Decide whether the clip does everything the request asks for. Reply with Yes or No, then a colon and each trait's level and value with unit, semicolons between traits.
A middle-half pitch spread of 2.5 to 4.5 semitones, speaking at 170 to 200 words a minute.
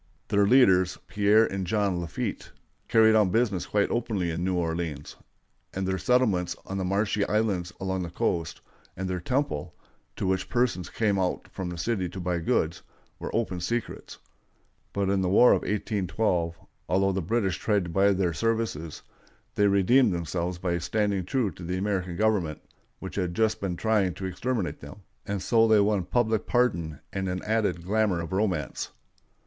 Yes: average, 3.4 semitones; average, 175 wpm